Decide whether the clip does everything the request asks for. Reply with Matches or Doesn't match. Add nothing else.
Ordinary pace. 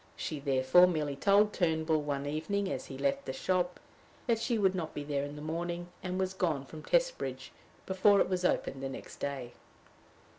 Matches